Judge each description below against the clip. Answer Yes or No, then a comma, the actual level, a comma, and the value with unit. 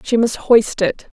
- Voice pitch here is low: No, high, 225 Hz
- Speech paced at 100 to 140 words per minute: No, average, 200 wpm